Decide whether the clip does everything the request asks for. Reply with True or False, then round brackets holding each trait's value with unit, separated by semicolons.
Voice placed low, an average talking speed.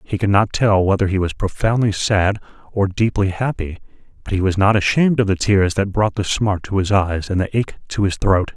False (100 Hz; 230 wpm)